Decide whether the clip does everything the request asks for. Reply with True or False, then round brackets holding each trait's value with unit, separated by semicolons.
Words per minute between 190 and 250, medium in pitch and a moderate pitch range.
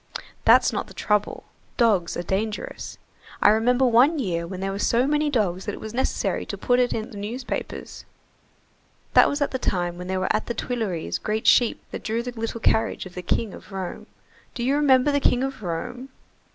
False (205 wpm; 225 Hz; 4.5 semitones)